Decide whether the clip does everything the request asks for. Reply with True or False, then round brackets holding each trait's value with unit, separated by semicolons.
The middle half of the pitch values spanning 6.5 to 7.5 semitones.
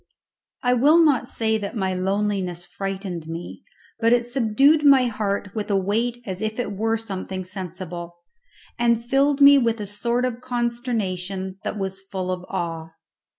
False (4.2 semitones)